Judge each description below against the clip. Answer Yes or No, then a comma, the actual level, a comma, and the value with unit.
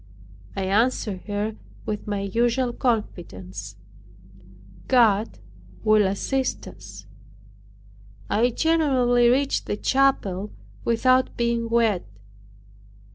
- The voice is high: Yes, high, 225 Hz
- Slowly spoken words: Yes, slow, 85 wpm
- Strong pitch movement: No, average, 3.9 semitones